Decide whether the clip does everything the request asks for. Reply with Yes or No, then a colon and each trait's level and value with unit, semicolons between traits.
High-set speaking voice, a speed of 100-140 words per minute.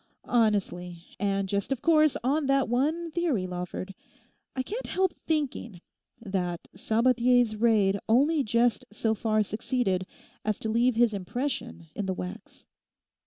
Yes: high, 225 Hz; slow, 135 wpm